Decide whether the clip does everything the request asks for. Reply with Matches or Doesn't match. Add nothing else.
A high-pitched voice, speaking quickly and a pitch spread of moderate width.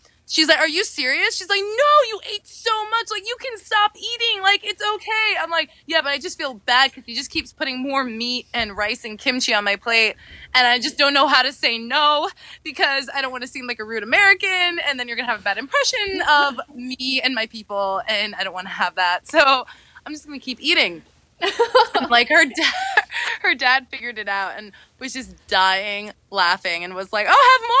Doesn't match